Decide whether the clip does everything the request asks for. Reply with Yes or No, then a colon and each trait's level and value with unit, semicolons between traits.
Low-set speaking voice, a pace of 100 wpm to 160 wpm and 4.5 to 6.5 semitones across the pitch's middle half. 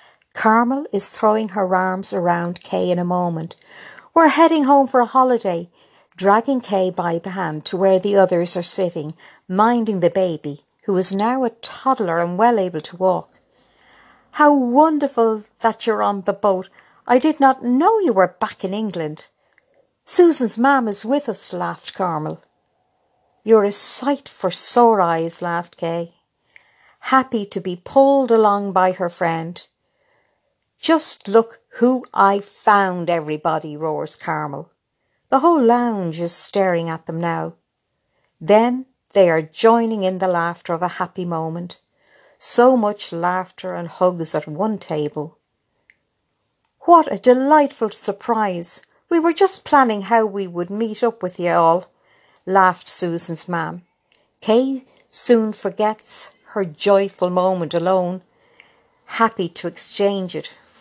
No: high, 195 Hz; average, 140 wpm; average, 5.1 semitones